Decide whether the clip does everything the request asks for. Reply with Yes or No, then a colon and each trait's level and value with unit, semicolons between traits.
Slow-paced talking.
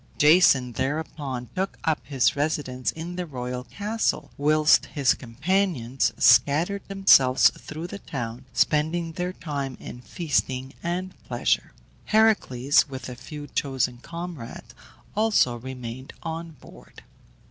Yes: slow, 120 wpm